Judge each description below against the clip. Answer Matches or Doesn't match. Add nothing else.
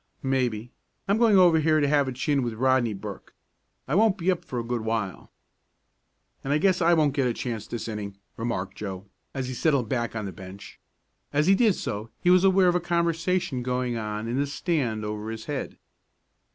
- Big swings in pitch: Matches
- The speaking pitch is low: Matches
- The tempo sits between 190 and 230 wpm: Matches